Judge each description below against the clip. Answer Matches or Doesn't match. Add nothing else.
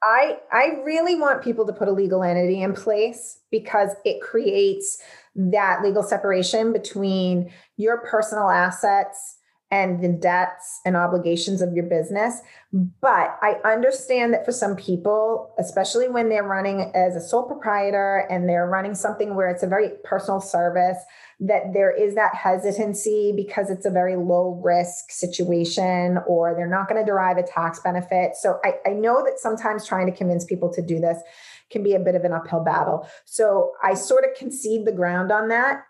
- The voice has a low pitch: Doesn't match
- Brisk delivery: Doesn't match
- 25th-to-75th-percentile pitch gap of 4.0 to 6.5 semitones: Doesn't match